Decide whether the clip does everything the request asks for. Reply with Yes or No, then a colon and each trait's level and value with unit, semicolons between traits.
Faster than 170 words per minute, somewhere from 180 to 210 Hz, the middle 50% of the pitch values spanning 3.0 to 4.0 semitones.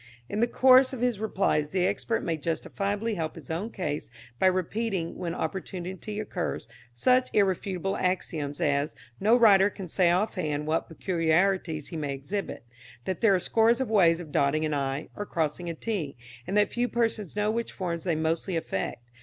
No: average, 180 wpm; medium, 185 Hz; average, 4.6 semitones